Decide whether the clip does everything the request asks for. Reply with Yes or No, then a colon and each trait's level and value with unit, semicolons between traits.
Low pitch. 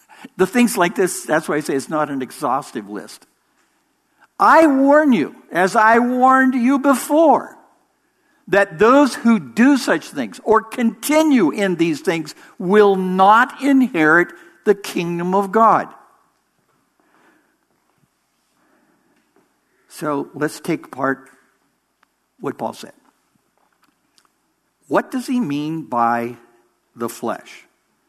No: high, 220 Hz